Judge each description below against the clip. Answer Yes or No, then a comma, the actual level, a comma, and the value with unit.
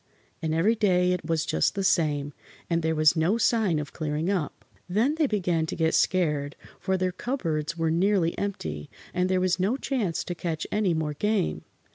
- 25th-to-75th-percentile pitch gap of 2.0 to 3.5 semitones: No, average, 3.9 semitones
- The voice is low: No, medium, 175 Hz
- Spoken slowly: No, average, 190 wpm